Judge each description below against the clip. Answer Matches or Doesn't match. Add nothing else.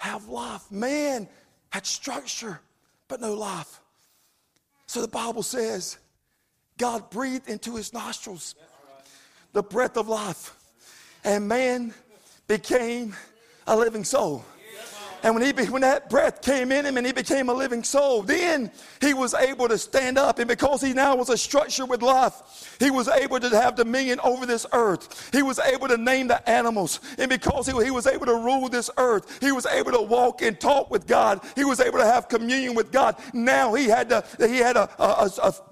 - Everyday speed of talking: Matches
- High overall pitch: Matches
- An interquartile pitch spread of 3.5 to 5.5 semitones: Doesn't match